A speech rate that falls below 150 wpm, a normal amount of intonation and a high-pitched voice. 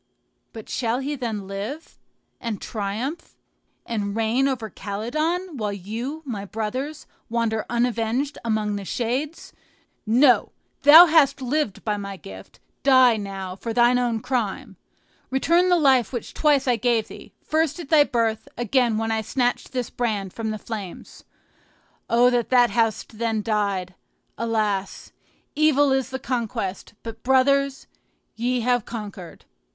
Yes: average, 140 wpm; average, 3.8 semitones; high, 235 Hz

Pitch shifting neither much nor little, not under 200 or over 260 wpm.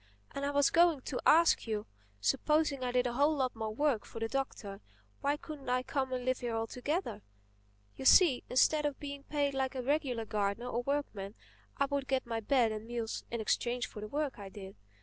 Yes: average, 4.0 semitones; fast, 205 wpm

